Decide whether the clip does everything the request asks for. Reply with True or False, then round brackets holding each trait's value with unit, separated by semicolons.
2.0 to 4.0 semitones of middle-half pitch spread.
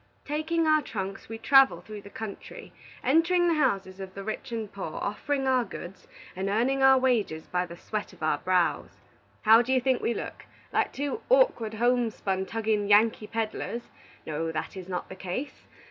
False (5.5 semitones)